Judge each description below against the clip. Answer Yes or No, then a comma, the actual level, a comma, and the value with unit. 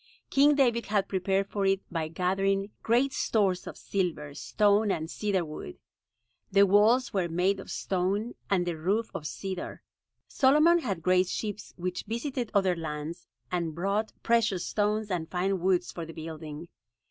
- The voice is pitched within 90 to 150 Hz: No, high, 195 Hz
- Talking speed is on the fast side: No, average, 160 wpm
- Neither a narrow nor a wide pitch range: Yes, average, 3.3 semitones